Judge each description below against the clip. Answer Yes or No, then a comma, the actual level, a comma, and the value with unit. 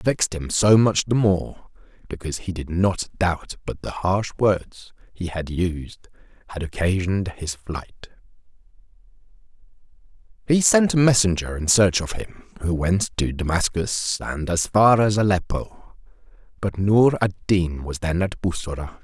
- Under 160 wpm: Yes, average, 150 wpm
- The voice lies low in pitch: Yes, very low, 95 Hz